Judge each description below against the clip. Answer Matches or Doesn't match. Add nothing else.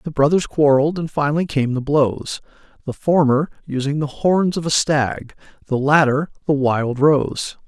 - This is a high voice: Doesn't match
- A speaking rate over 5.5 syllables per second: Doesn't match